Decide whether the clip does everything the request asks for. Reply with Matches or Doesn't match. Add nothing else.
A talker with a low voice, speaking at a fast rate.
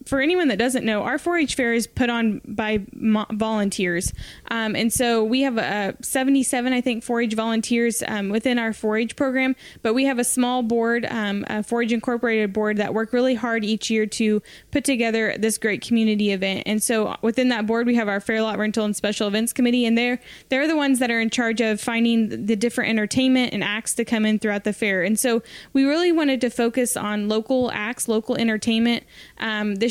Doesn't match